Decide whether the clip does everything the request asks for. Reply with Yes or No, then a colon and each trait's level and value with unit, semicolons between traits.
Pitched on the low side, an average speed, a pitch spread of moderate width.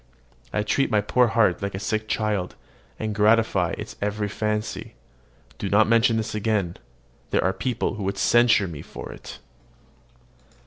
No: low, 105 Hz; average, 160 wpm; narrow, 2.0 semitones